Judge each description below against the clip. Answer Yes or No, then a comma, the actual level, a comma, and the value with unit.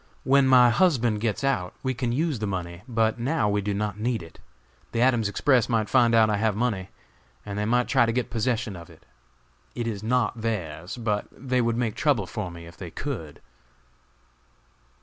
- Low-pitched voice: Yes, low, 115 Hz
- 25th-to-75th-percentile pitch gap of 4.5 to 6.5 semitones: No, average, 3.3 semitones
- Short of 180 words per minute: No, average, 195 wpm